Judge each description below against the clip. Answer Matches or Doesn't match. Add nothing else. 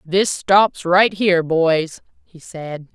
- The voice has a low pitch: Doesn't match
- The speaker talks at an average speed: Matches